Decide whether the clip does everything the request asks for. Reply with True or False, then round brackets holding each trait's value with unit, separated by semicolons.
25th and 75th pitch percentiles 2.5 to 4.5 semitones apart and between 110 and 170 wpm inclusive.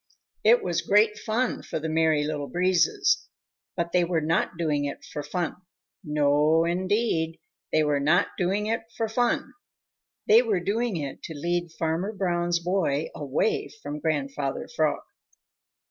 False (5.0 semitones; 145 wpm)